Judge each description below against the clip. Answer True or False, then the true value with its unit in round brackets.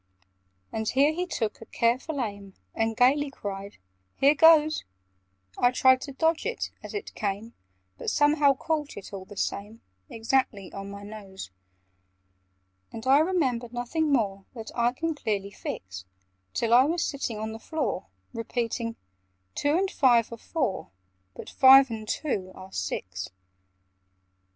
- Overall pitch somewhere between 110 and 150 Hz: False (240 Hz)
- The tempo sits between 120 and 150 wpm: True (145 wpm)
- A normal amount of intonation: False (5.8 semitones)